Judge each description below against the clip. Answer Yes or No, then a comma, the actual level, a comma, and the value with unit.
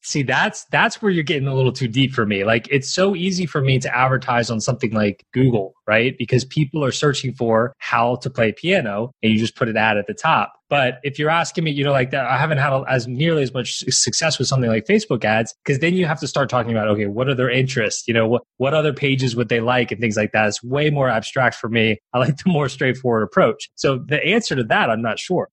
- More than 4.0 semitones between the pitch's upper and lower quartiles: No, average, 3.6 semitones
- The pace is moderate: No, fast, 260 wpm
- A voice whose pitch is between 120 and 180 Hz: Yes, low, 130 Hz